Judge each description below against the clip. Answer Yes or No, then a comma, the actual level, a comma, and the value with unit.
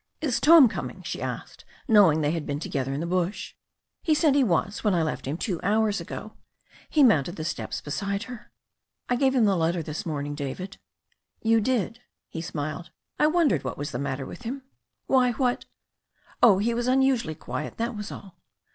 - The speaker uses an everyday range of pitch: No, wide, 7.6 semitones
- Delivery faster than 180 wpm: Yes, average, 200 wpm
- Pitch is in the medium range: No, high, 200 Hz